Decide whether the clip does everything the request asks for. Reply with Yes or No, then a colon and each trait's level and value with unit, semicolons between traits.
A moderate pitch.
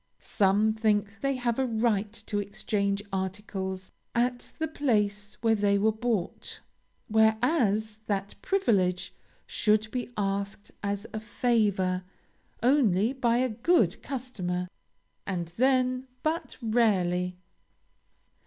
No: high, 215 Hz